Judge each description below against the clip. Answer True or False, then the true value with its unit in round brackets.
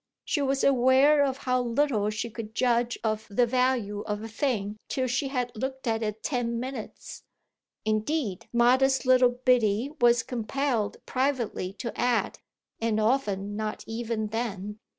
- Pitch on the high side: True (240 Hz)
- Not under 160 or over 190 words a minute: False (150 wpm)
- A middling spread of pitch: True (3.2 semitones)